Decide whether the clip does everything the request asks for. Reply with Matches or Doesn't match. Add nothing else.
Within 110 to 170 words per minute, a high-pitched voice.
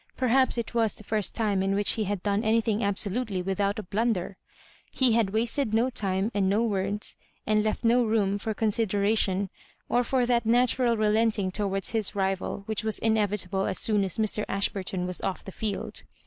Doesn't match